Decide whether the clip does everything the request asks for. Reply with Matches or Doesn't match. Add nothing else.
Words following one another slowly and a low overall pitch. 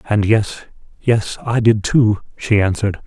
Matches